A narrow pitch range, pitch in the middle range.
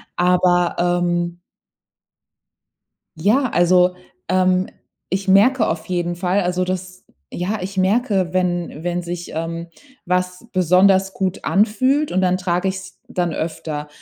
Yes: narrow, 1.6 semitones; medium, 180 Hz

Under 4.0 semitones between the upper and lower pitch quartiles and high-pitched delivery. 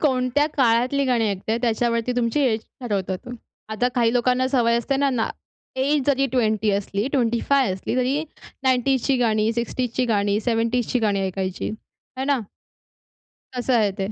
Yes: average, 3.0 semitones; high, 240 Hz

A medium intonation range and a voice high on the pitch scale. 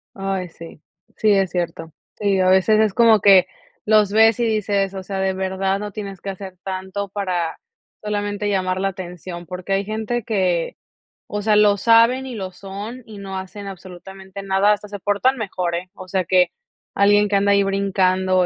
No: narrow, 1.8 semitones; high, 195 Hz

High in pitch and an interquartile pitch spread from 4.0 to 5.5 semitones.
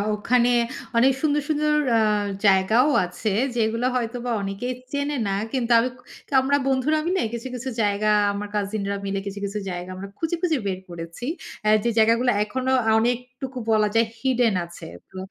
Yes: high, 235 Hz; average, 4.3 semitones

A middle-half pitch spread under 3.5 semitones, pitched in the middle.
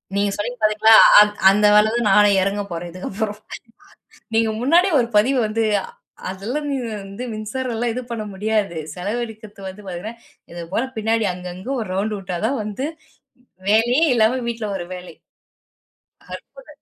No: average, 3.0 semitones; high, 215 Hz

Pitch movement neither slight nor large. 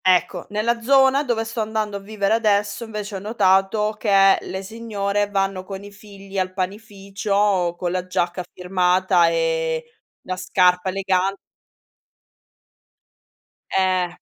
No: narrow, 2.3 semitones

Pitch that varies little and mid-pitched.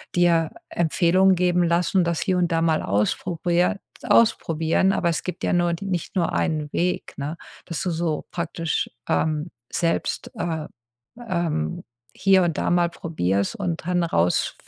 Yes: narrow, 1.9 semitones; medium, 170 Hz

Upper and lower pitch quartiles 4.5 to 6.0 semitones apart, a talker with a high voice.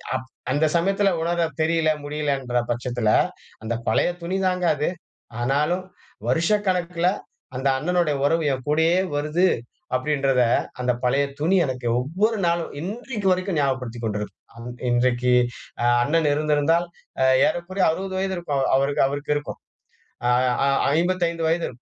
No: average, 4.8 semitones; medium, 155 Hz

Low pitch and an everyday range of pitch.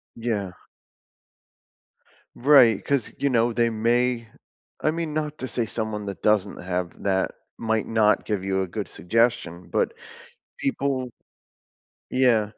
Yes: low, 115 Hz; average, 3.6 semitones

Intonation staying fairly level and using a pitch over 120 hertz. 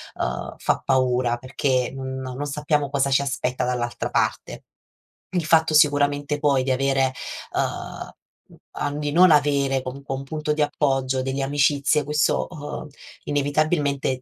Yes: narrow, 2.0 semitones; medium, 140 Hz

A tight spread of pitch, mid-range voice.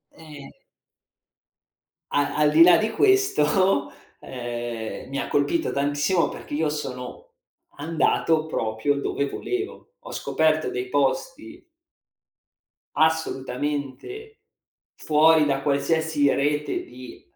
No: average, 3.1 semitones; medium, 150 Hz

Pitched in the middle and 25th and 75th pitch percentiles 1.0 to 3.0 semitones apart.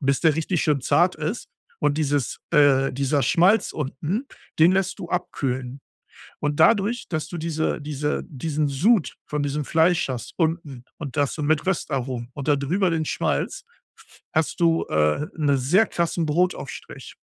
No: medium, 150 Hz; average, 3.6 semitones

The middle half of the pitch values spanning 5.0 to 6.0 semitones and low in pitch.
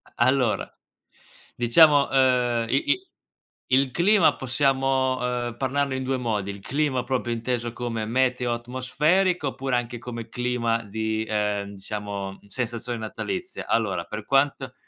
No: narrow, 2.6 semitones; low, 125 Hz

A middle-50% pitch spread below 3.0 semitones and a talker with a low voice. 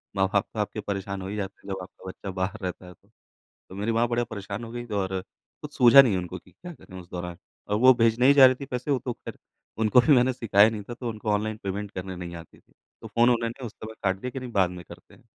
No: average, 3.9 semitones; low, 105 Hz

